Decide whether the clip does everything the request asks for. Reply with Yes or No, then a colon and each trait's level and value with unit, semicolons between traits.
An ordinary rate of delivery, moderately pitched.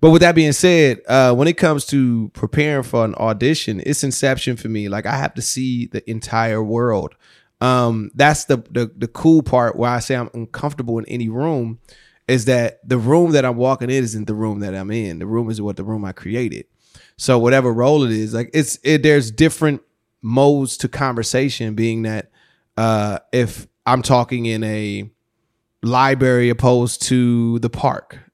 No: average, 190 wpm; low, 120 Hz